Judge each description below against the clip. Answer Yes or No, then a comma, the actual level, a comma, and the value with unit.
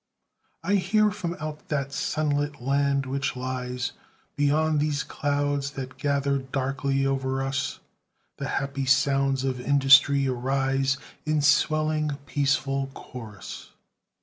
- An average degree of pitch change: No, narrow, 1.4 semitones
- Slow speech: Yes, slow, 115 wpm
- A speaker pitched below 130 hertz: No, medium, 140 Hz